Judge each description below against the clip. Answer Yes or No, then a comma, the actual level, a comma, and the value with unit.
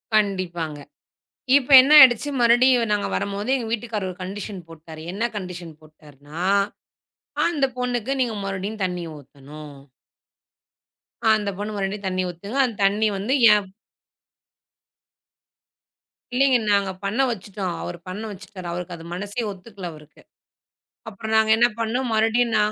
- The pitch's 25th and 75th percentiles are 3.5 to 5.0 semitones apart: Yes, average, 4.1 semitones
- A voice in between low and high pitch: No, high, 200 Hz